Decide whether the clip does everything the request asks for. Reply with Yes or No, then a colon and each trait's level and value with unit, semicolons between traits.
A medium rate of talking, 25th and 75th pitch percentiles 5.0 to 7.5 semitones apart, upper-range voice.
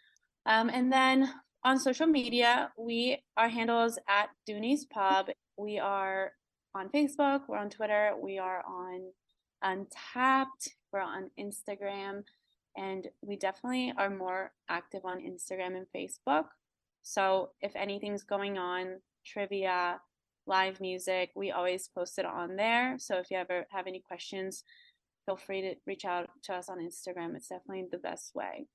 No: average, 150 wpm; average, 3.8 semitones; high, 195 Hz